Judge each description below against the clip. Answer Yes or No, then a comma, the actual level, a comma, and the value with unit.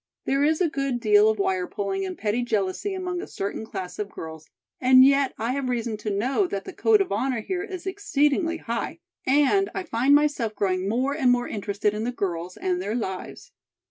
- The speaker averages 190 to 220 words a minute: Yes, fast, 205 wpm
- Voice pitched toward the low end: No, high, 240 Hz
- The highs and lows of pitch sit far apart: Yes, wide, 6.3 semitones